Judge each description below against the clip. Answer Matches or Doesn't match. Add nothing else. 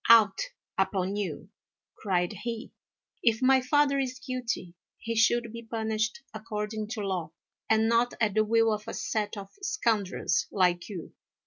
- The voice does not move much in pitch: Matches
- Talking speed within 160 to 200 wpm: Doesn't match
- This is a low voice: Doesn't match